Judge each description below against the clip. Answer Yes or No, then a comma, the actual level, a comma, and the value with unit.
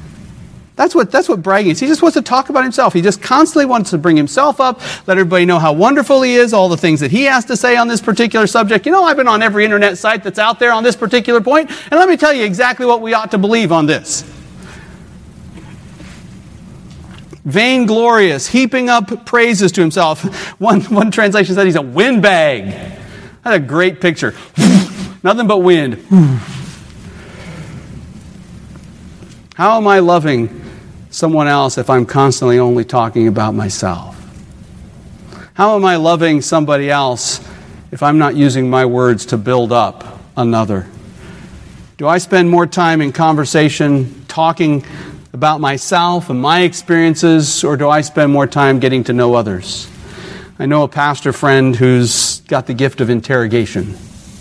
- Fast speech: No, average, 165 wpm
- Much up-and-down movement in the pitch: Yes, wide, 8.1 semitones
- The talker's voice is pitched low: No, medium, 175 Hz